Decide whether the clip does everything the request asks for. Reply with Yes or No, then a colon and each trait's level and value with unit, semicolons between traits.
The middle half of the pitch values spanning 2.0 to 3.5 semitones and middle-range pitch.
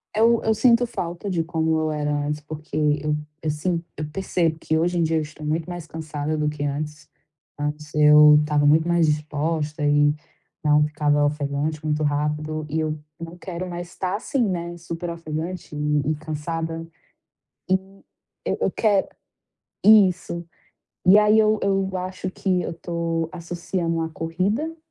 Yes: average, 2.8 semitones; medium, 160 Hz